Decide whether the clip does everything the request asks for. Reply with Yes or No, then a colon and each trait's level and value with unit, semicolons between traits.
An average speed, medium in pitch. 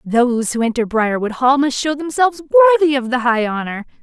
No: average, 195 wpm; very high, 260 Hz